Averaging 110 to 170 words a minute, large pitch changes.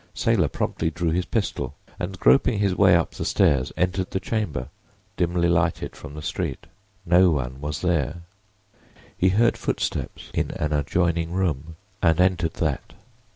No: average, 155 wpm; average, 3.3 semitones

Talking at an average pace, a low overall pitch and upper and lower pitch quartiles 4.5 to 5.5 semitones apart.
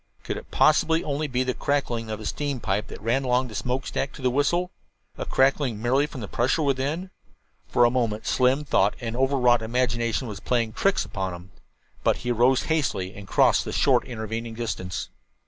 No: average, 195 wpm; low, 125 Hz; average, 3.5 semitones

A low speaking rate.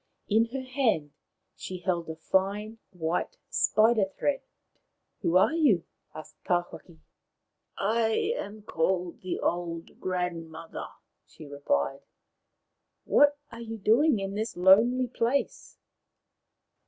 Yes: slow, 115 wpm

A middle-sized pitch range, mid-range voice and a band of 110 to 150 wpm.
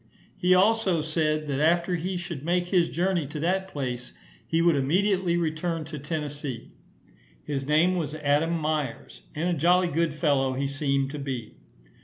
No: average, 3.5 semitones; medium, 155 Hz; average, 165 wpm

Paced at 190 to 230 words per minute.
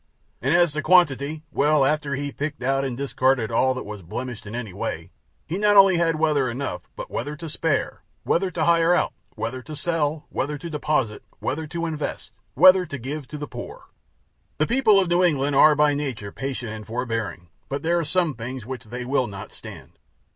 Yes: average, 200 wpm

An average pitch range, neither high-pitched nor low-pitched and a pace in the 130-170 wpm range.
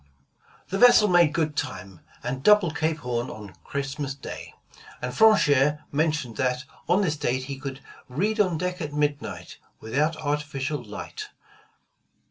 Yes: average, 4.1 semitones; medium, 150 Hz; average, 140 wpm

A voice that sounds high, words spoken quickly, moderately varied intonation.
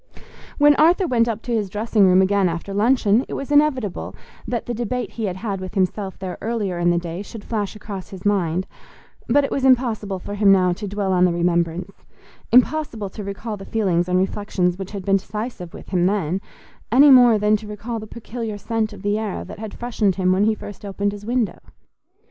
Yes: high, 205 Hz; fast, 210 wpm; average, 3.4 semitones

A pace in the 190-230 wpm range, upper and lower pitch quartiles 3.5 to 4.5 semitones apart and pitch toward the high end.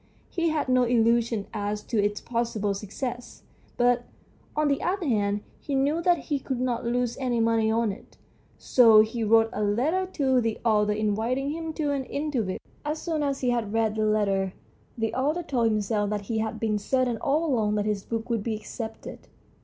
Yes: average, 195 wpm; average, 4.0 semitones; high, 230 Hz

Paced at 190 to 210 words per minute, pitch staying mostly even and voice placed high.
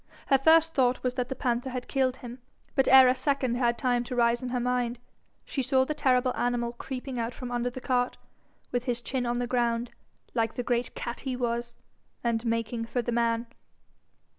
Yes: fast, 205 wpm; narrow, 1.4 semitones; high, 245 Hz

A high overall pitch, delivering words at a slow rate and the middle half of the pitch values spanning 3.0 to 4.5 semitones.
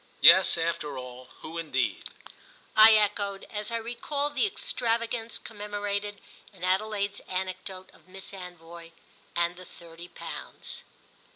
Yes: high, 195 Hz; slow, 120 wpm; average, 3.9 semitones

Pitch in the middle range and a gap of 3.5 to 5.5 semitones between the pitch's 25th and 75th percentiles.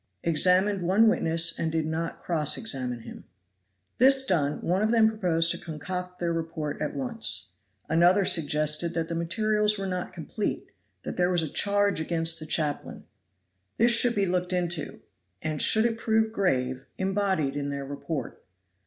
Yes: medium, 175 Hz; average, 4.4 semitones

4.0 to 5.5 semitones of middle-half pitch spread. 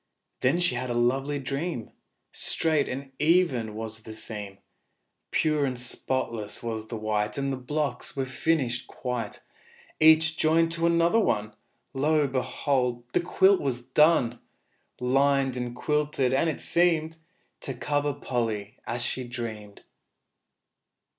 Yes: average, 4.3 semitones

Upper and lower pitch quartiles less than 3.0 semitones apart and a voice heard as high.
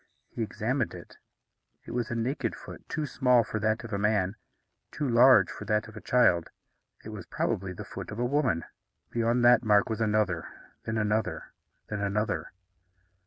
No: narrow, 2.5 semitones; low, 110 Hz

